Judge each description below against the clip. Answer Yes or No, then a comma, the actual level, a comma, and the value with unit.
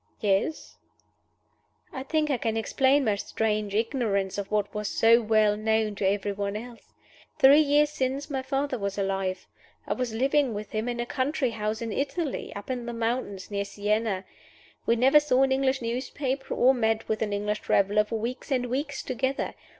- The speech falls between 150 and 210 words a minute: Yes, average, 180 wpm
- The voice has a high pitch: Yes, high, 230 Hz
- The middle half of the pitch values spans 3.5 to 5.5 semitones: Yes, average, 4.0 semitones